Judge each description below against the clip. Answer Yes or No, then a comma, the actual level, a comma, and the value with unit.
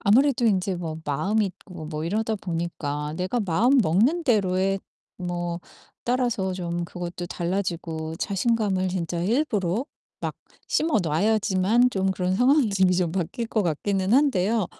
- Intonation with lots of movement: No, average, 4.3 semitones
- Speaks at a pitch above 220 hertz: No, high, 190 Hz